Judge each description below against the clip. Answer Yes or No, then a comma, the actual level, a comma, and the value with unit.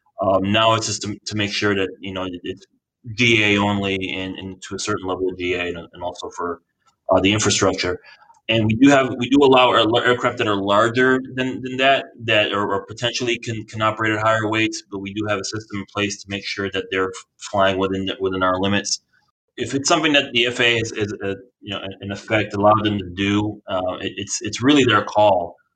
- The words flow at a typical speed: No, fast, 220 wpm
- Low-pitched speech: Yes, low, 105 Hz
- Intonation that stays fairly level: No, average, 3.0 semitones